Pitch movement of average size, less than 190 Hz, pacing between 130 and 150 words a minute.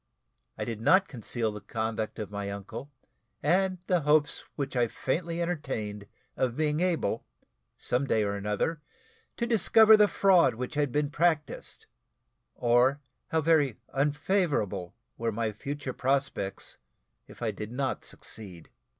No: wide, 6.4 semitones; low, 135 Hz; average, 140 wpm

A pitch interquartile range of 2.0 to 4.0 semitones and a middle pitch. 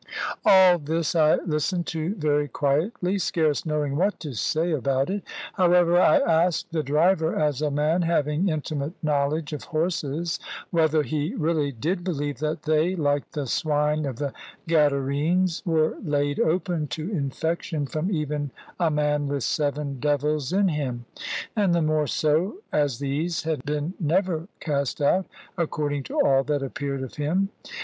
Yes: average, 2.8 semitones; medium, 155 Hz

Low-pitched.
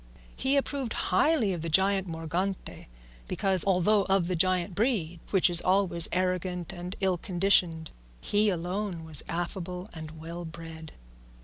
No: medium, 180 Hz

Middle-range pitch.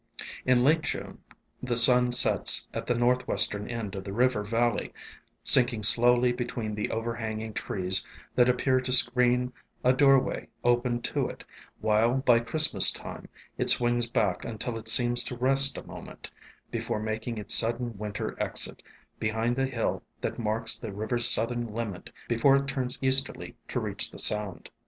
No: low, 120 Hz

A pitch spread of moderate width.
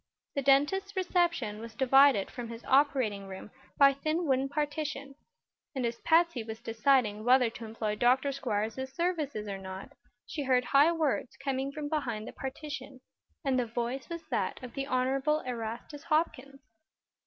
Yes: average, 3.9 semitones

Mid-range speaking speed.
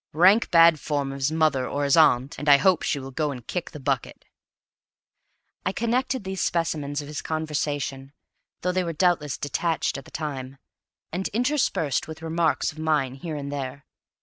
Yes: average, 180 wpm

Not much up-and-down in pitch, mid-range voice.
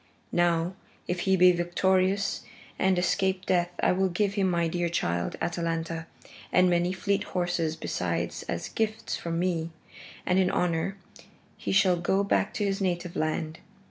Yes: narrow, 2.0 semitones; medium, 180 Hz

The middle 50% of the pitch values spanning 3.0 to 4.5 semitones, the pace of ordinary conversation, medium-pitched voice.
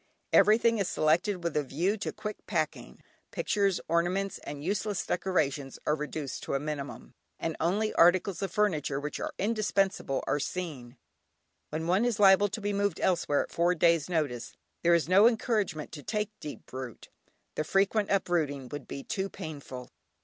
No: average, 5.1 semitones; average, 165 wpm; medium, 175 Hz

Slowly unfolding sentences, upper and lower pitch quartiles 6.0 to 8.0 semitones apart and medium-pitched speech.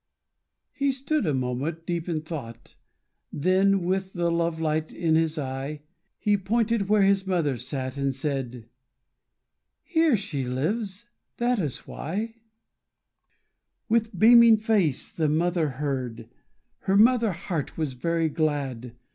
Yes: slow, 130 wpm; wide, 6.4 semitones; medium, 165 Hz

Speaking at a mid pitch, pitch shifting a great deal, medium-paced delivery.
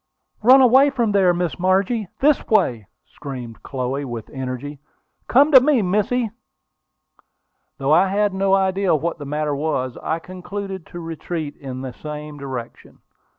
Yes: medium, 175 Hz; wide, 6.3 semitones; average, 150 wpm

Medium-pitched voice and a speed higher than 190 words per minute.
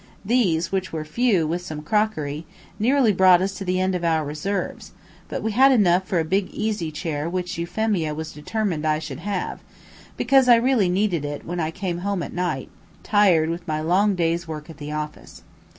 Yes: medium, 180 Hz; average, 200 wpm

